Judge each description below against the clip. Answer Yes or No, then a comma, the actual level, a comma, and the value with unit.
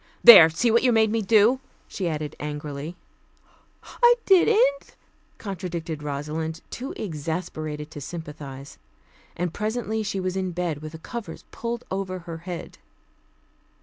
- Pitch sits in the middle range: Yes, medium, 180 Hz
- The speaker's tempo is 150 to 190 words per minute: No, slow, 135 wpm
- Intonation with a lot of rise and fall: Yes, wide, 6.0 semitones